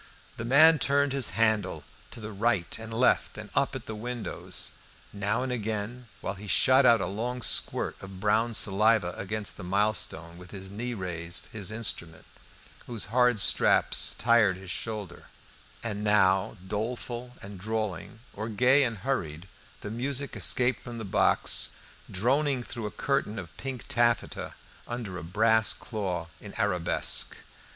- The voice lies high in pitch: No, low, 110 Hz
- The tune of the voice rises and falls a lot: No, average, 3.6 semitones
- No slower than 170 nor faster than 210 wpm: No, average, 155 wpm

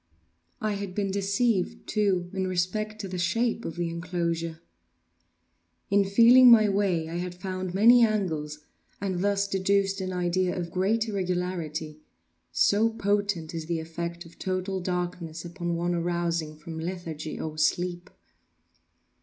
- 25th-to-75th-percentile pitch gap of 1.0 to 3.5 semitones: Yes, average, 2.8 semitones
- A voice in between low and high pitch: Yes, medium, 180 Hz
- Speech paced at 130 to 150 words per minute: Yes, average, 140 wpm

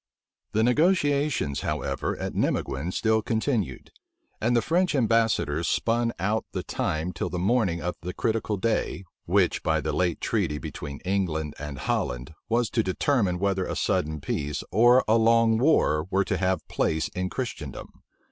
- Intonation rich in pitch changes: Yes, wide, 6.2 semitones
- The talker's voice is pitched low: Yes, low, 100 Hz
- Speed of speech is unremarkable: Yes, average, 155 wpm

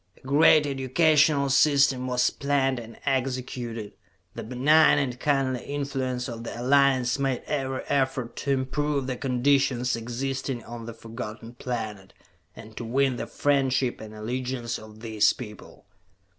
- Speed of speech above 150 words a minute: No, average, 140 wpm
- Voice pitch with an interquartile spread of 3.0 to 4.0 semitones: No, narrow, 2.6 semitones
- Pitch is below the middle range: Yes, low, 130 Hz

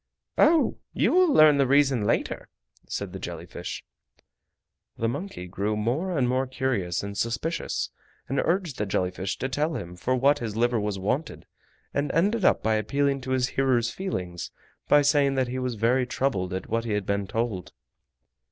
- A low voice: Yes, low, 125 Hz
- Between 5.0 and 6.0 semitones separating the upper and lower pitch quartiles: Yes, average, 5.3 semitones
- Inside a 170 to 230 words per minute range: Yes, average, 180 wpm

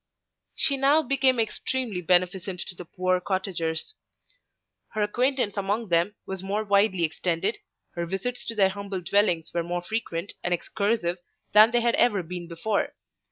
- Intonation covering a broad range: No, average, 3.9 semitones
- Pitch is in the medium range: No, high, 195 Hz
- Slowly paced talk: No, average, 155 wpm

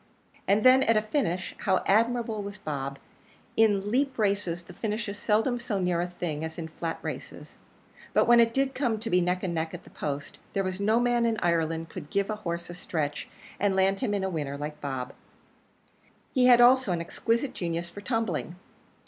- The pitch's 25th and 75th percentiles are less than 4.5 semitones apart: No, average, 5.2 semitones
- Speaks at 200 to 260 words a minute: Yes, fast, 205 wpm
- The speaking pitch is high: Yes, high, 195 Hz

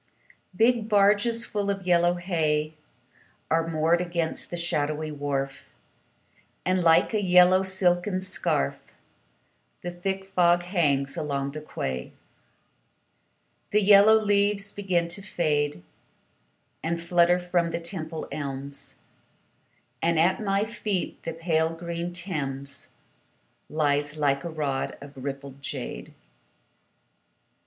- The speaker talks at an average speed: No, slow, 115 wpm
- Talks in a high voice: No, medium, 170 Hz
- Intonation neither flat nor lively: Yes, average, 4.0 semitones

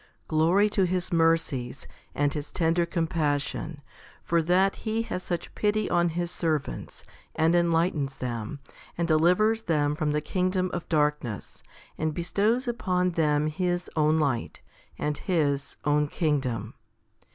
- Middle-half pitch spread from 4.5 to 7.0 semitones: No, average, 3.3 semitones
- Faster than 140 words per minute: No, slow, 135 wpm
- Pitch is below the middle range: No, medium, 165 Hz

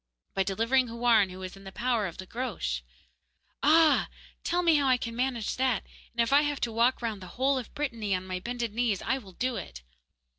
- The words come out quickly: Yes, fast, 220 wpm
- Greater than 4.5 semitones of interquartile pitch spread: Yes, average, 4.9 semitones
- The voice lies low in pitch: No, high, 235 Hz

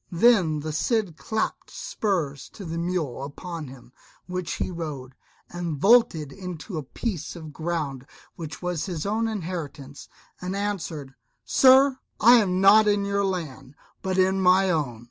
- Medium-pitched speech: Yes, medium, 175 Hz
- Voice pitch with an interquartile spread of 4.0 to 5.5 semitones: Yes, average, 4.6 semitones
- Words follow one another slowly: No, average, 145 wpm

